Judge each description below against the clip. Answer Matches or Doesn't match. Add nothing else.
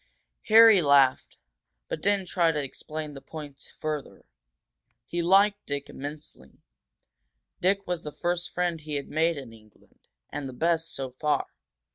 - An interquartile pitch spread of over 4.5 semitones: Doesn't match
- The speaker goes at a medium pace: Matches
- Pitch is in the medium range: Matches